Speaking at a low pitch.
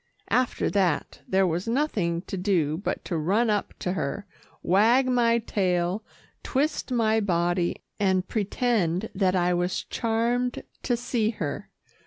No: high, 200 Hz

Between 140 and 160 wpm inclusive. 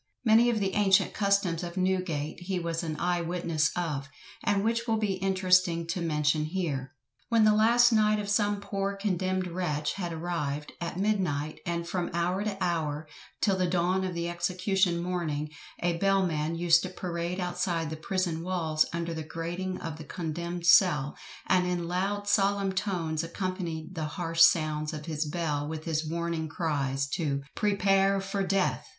No: average, 170 wpm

